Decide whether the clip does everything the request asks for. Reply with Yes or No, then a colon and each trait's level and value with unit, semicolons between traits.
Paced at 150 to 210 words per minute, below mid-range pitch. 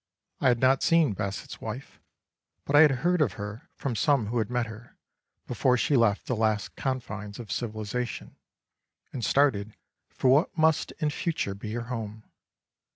Yes: average, 165 wpm; low, 120 Hz